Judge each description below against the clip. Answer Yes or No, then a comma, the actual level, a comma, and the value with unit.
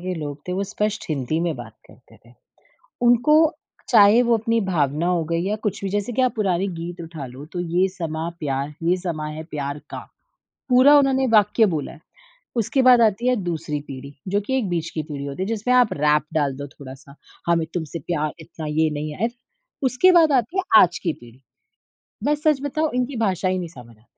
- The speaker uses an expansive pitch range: Yes, wide, 7.1 semitones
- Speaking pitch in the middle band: Yes, medium, 175 Hz